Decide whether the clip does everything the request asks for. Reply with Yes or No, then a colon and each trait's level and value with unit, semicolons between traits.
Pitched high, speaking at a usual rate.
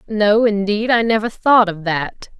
Yes: high, 210 Hz; average, 175 wpm